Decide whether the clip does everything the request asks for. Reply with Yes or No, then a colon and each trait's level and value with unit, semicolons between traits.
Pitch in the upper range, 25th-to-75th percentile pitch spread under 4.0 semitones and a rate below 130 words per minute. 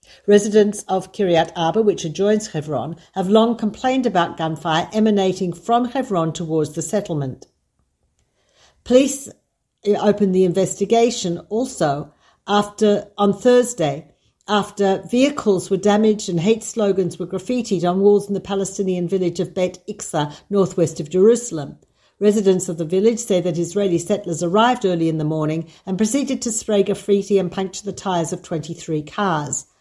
No: high, 195 Hz; average, 3.6 semitones; average, 145 wpm